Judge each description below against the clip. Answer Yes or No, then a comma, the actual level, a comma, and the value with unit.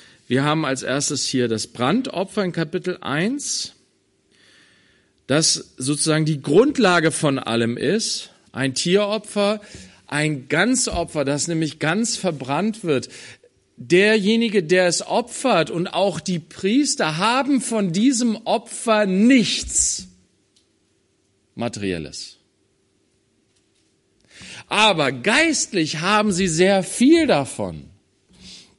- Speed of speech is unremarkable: No, slow, 100 wpm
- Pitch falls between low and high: Yes, medium, 170 Hz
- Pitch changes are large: Yes, wide, 8.1 semitones